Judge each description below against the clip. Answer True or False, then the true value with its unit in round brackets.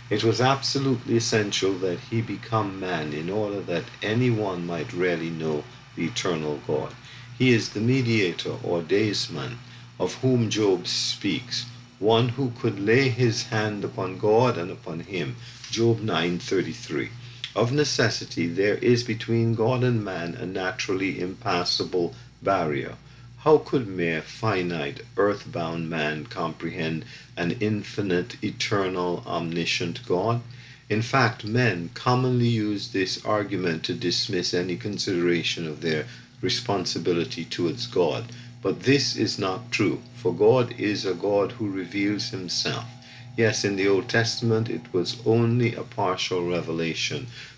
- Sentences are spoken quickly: False (135 wpm)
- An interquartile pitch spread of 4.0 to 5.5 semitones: True (4.7 semitones)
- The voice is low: True (110 Hz)